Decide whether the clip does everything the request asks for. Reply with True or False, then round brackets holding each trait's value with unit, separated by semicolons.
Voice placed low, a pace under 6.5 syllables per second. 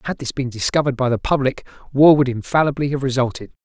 False (130 Hz; 6.8 syllables/s)